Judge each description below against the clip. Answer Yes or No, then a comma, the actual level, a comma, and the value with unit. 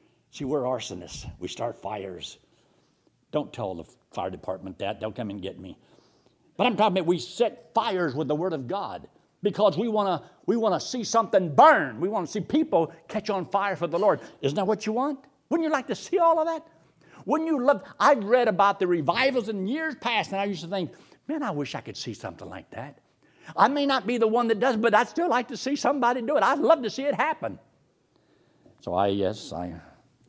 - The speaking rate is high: Yes, fast, 225 wpm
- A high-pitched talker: Yes, high, 210 Hz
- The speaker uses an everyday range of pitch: No, wide, 7.8 semitones